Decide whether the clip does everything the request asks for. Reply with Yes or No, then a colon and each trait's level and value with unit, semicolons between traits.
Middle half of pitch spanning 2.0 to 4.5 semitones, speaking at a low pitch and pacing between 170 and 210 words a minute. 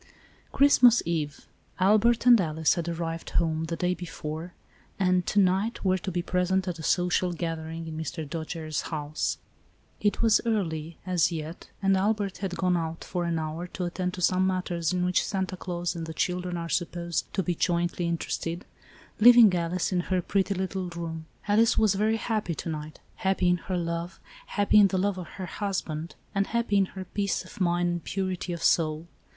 No: narrow, 2.4 semitones; medium, 180 Hz; average, 190 wpm